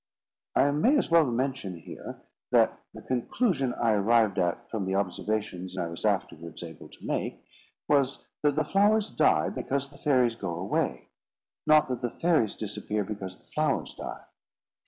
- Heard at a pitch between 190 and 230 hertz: No, low, 120 Hz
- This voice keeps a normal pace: Yes, average, 160 wpm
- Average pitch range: No, wide, 6.7 semitones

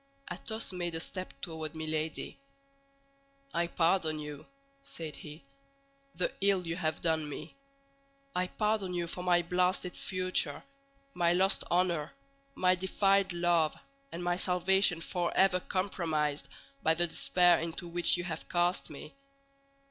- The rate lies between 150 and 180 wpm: No, slow, 135 wpm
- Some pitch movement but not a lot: No, narrow, 2.1 semitones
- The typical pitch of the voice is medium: Yes, medium, 175 Hz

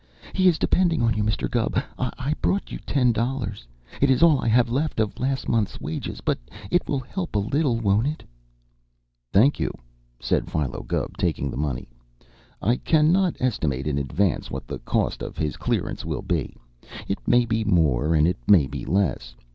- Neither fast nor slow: Yes, average, 185 wpm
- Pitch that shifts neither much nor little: No, wide, 8.2 semitones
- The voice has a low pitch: Yes, low, 115 Hz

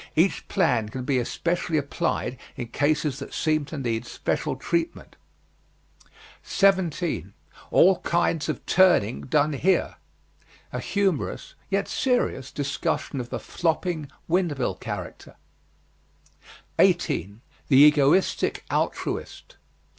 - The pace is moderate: No, slow, 110 wpm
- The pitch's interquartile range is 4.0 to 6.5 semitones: Yes, average, 5.0 semitones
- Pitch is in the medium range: Yes, medium, 150 Hz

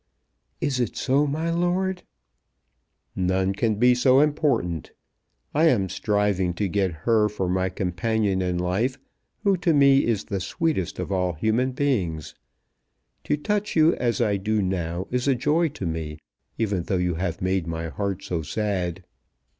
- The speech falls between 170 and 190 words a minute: No, average, 160 wpm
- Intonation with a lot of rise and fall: Yes, wide, 6.8 semitones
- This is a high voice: No, low, 105 Hz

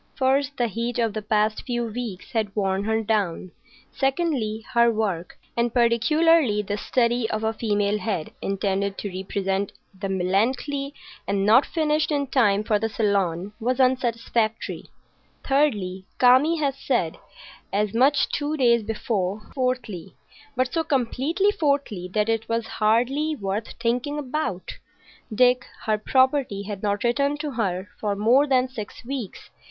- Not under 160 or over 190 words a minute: No, average, 140 wpm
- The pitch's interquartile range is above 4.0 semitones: Yes, average, 4.4 semitones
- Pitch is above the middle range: Yes, high, 230 Hz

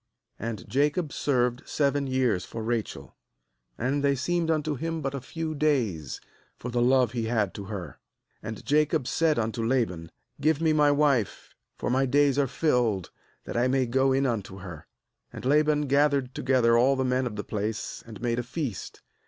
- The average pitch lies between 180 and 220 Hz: No, low, 130 Hz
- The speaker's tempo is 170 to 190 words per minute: Yes, average, 180 wpm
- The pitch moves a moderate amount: Yes, average, 4.0 semitones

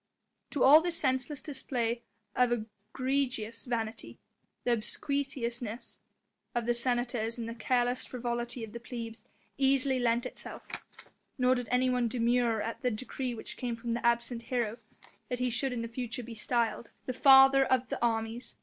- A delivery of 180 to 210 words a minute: No, average, 155 wpm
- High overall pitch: Yes, high, 240 Hz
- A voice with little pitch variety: Yes, narrow, 1.8 semitones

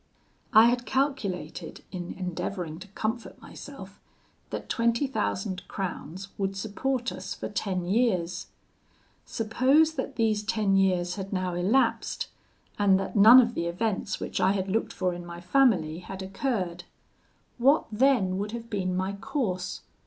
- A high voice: Yes, high, 195 Hz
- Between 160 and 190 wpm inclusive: No, average, 145 wpm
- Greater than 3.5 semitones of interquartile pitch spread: Yes, average, 4.2 semitones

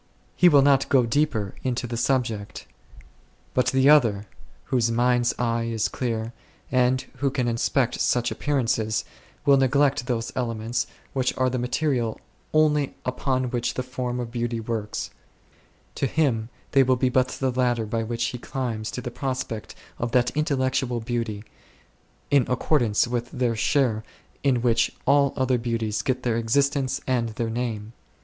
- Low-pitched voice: Yes, low, 125 Hz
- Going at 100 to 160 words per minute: Yes, average, 155 wpm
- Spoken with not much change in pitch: Yes, narrow, 2.2 semitones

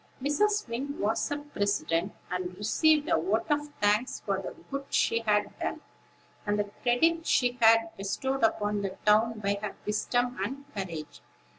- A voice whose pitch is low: No, high, 225 Hz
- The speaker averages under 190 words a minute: Yes, average, 155 wpm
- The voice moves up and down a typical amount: Yes, average, 4.9 semitones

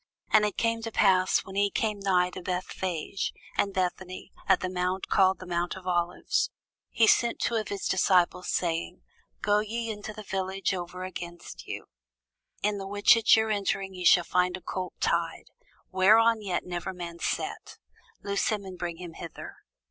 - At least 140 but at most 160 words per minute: No, average, 180 wpm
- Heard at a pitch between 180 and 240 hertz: Yes, high, 190 Hz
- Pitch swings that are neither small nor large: No, narrow, 2.3 semitones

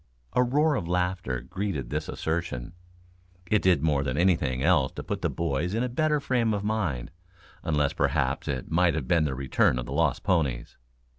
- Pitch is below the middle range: Yes, very low, 85 Hz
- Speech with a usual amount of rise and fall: No, wide, 6.5 semitones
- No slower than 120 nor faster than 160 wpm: No, average, 190 wpm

